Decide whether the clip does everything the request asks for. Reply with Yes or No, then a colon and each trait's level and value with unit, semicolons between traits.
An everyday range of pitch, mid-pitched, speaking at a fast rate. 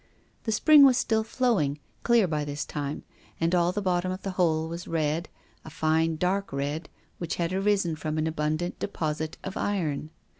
No: average, 3.8 semitones; medium, 170 Hz; average, 180 wpm